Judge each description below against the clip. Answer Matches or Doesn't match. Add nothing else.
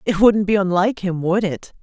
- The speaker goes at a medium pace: Doesn't match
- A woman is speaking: Matches